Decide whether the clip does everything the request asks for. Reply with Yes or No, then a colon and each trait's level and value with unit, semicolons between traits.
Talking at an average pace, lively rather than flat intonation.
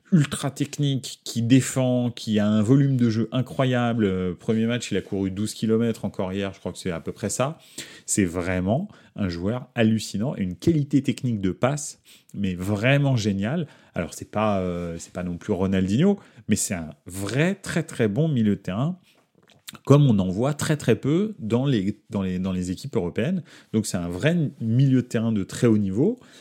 Yes: average, 195 wpm; wide, 5.9 semitones